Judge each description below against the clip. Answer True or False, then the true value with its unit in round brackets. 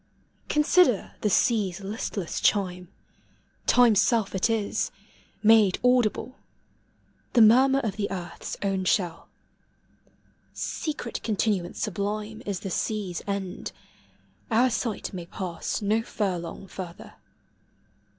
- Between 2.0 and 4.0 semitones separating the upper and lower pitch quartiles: True (3.3 semitones)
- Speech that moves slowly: True (110 wpm)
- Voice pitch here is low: False (205 Hz)